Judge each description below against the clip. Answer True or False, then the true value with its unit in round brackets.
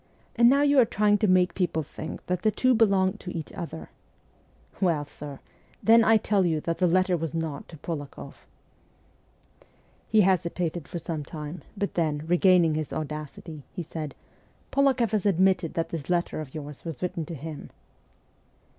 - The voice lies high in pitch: False (175 Hz)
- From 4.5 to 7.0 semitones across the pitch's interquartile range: False (3.8 semitones)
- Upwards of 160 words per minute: True (170 wpm)